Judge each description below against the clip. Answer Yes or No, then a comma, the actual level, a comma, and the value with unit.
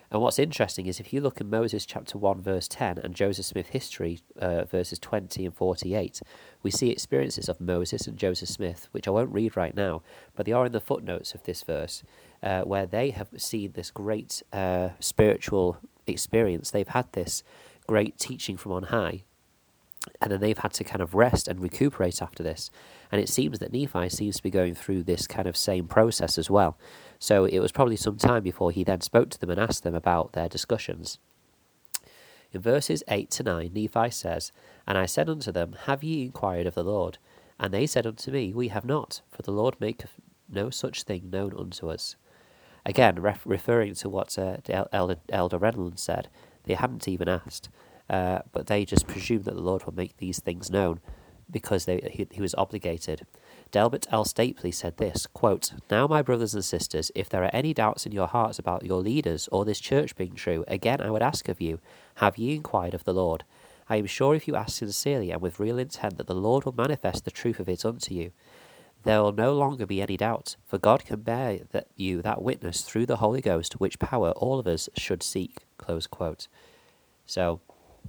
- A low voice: Yes, low, 100 Hz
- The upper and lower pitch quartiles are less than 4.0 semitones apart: Yes, average, 3.6 semitones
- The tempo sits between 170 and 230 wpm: Yes, fast, 205 wpm